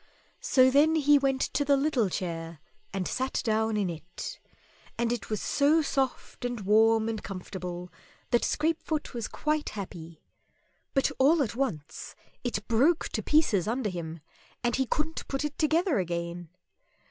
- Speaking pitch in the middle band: No, high, 235 Hz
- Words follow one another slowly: No, average, 155 wpm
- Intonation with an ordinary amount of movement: No, wide, 7.3 semitones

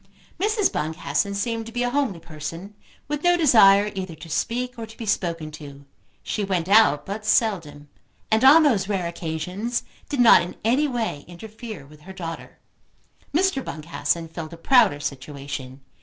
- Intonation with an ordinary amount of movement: No, wide, 6.6 semitones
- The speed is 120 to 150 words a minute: No, average, 165 wpm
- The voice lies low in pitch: No, high, 195 Hz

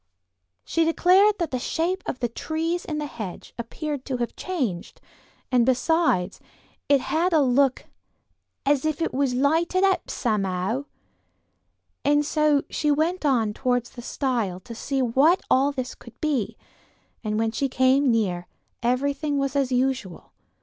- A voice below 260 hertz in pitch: No, very high, 275 Hz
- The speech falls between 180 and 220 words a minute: No, average, 155 wpm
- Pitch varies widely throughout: No, average, 4.3 semitones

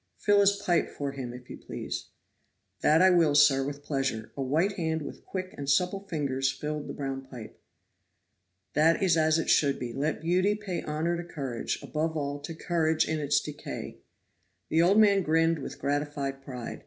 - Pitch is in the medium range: Yes, medium, 150 Hz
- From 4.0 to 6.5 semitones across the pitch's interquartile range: No, average, 3.6 semitones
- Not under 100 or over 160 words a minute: No, average, 185 wpm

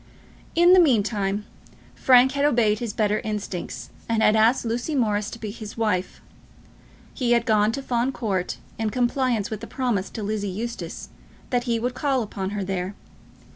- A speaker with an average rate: Yes, average, 175 wpm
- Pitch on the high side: Yes, high, 225 Hz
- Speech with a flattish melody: No, average, 3.1 semitones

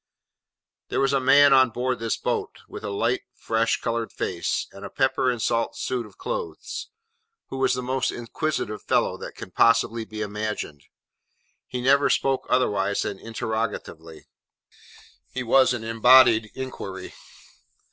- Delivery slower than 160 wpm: Yes, average, 145 wpm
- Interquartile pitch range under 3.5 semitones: Yes, average, 3.1 semitones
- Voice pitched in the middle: No, low, 115 Hz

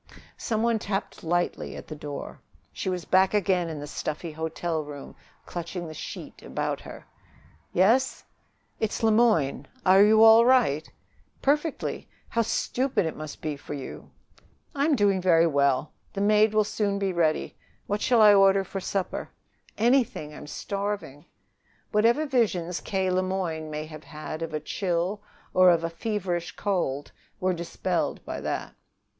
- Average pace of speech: Yes, average, 155 wpm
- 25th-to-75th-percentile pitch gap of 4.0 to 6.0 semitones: Yes, average, 4.8 semitones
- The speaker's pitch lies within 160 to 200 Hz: Yes, medium, 185 Hz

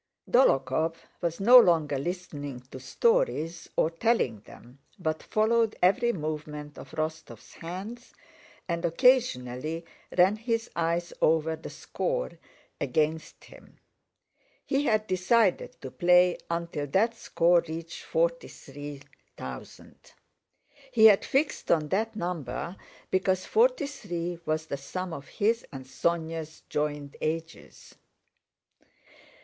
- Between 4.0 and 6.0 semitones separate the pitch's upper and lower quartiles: Yes, wide, 5.6 semitones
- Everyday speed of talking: No, slow, 115 wpm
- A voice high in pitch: No, medium, 170 Hz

